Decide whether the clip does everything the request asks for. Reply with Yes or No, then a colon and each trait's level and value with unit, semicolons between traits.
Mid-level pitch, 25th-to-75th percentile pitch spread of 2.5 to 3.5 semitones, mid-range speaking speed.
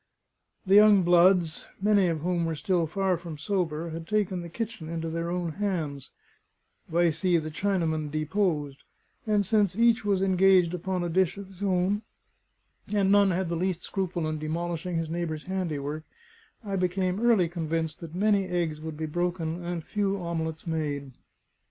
Yes: medium, 175 Hz; average, 3.1 semitones; average, 165 wpm